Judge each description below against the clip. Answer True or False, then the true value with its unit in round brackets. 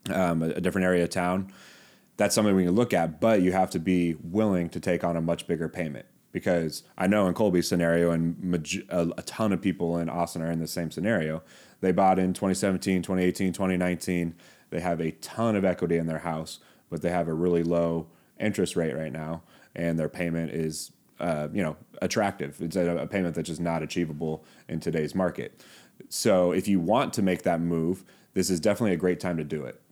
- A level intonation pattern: True (2.0 semitones)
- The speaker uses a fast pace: True (215 wpm)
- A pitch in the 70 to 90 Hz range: True (85 Hz)